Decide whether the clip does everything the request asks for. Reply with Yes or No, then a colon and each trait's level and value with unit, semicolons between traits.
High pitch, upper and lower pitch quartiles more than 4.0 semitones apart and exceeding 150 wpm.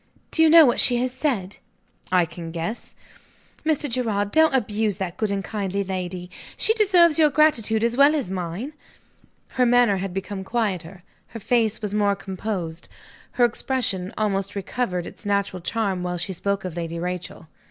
Yes: high, 205 Hz; average, 4.9 semitones; average, 170 wpm